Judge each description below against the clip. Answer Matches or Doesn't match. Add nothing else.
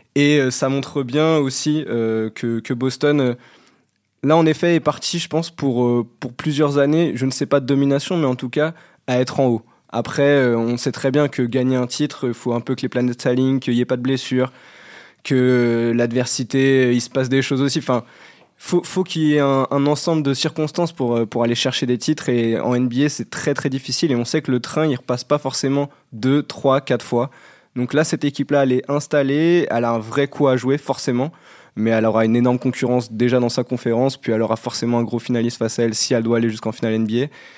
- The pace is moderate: Doesn't match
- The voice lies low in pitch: Matches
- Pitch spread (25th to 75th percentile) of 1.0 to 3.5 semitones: Matches